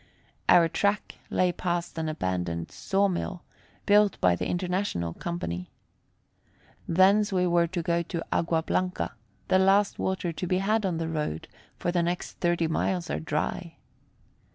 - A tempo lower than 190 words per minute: Yes, average, 155 wpm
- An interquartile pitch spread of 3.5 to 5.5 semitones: No, narrow, 2.5 semitones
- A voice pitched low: No, medium, 175 Hz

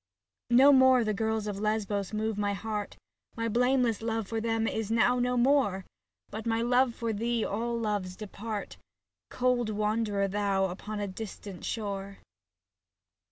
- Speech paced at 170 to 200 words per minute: No, average, 150 wpm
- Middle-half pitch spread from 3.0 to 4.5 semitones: No, narrow, 2.4 semitones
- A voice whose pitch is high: Yes, high, 220 Hz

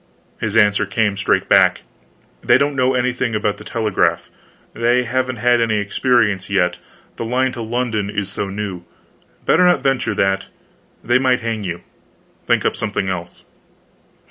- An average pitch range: Yes, average, 3.8 semitones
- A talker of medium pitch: No, low, 110 Hz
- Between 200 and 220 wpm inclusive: No, average, 155 wpm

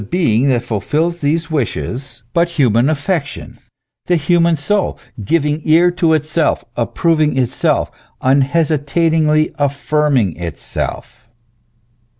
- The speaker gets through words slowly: Yes, slow, 105 wpm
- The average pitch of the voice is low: No, medium, 150 Hz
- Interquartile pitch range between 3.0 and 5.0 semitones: Yes, average, 3.8 semitones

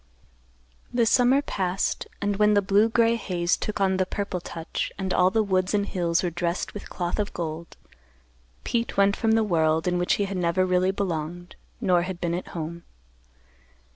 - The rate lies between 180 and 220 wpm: Yes, average, 185 wpm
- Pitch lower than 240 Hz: Yes, medium, 185 Hz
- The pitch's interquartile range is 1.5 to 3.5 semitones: Yes, average, 2.9 semitones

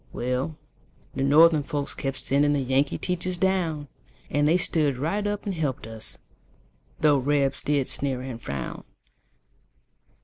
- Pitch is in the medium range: Yes, medium, 145 Hz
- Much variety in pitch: No, average, 3.4 semitones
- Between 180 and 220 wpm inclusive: No, average, 140 wpm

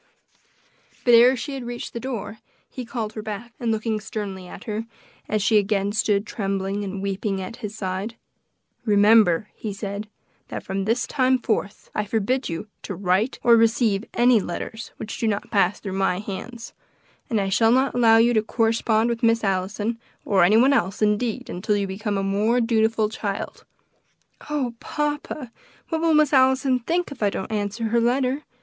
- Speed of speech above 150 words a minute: Yes, average, 180 wpm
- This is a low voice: No, high, 220 Hz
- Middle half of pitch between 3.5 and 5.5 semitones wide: No, average, 3.1 semitones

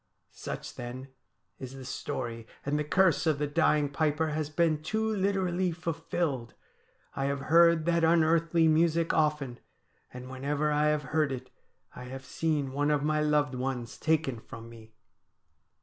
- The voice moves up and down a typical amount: Yes, average, 3.5 semitones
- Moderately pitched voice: Yes, medium, 150 Hz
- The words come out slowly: No, average, 160 wpm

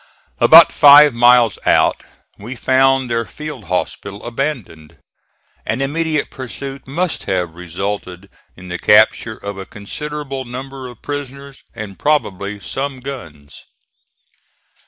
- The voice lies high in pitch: No, low, 125 Hz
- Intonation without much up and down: No, wide, 5.6 semitones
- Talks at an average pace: No, slow, 115 wpm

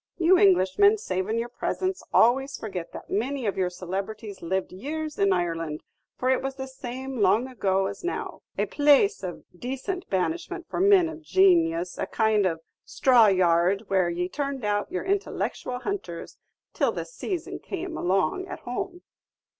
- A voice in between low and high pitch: No, very high, 250 Hz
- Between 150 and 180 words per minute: Yes, average, 160 wpm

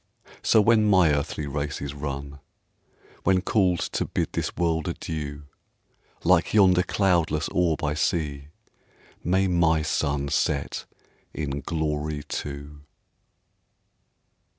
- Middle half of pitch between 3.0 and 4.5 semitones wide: Yes, average, 3.8 semitones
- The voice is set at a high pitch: No, very low, 80 Hz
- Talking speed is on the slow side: Yes, slow, 110 wpm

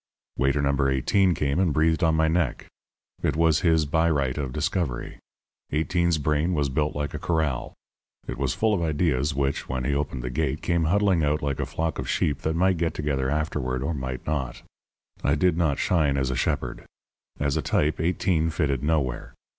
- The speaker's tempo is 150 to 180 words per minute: No, average, 195 wpm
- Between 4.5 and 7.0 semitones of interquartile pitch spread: No, average, 3.1 semitones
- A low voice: Yes, very low, 75 Hz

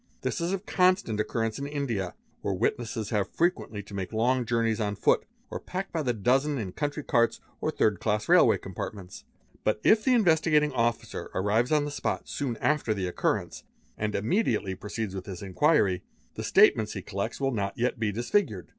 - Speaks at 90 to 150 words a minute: No, average, 190 wpm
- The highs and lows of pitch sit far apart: Yes, wide, 6.0 semitones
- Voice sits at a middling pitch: No, low, 115 Hz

